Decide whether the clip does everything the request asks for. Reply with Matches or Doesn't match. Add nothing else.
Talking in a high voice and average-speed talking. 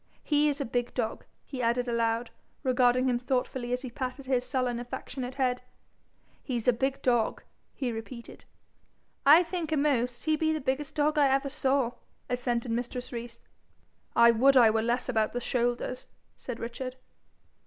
Matches